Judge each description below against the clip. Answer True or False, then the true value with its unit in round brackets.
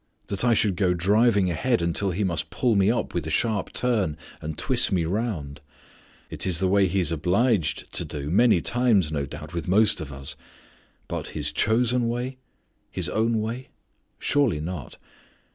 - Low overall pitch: True (95 Hz)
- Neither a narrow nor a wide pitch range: False (5.8 semitones)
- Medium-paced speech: True (180 wpm)